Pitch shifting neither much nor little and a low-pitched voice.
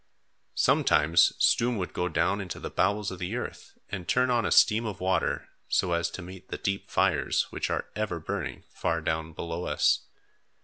Yes: average, 3.6 semitones; very low, 95 Hz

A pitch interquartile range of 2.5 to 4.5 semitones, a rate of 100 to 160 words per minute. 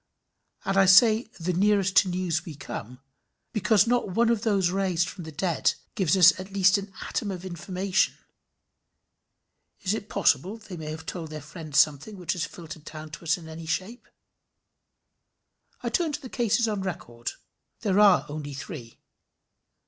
No: average, 4.0 semitones; average, 170 wpm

